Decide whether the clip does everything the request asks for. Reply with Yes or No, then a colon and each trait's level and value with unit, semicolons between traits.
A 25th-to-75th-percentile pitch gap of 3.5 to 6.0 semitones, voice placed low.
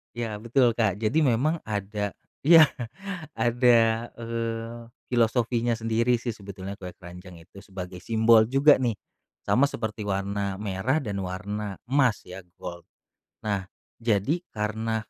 No: average, 3.0 semitones; low, 110 Hz